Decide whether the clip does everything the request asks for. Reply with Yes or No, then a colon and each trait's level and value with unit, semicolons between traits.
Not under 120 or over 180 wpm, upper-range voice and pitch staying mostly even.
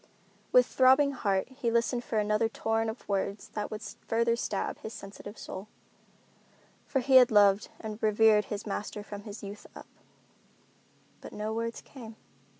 Yes: average, 160 wpm; high, 220 Hz; narrow, 2.1 semitones